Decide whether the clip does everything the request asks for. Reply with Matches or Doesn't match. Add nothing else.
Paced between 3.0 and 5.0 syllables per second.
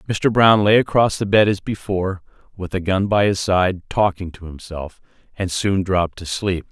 Matches